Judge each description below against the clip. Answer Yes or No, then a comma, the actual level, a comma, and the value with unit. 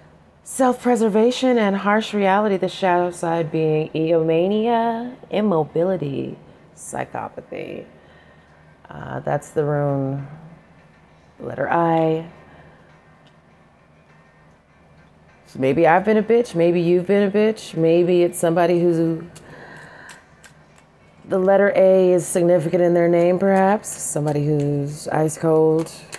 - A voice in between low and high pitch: Yes, medium, 170 Hz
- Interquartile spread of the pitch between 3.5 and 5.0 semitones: Yes, average, 4.0 semitones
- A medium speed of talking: No, slow, 105 wpm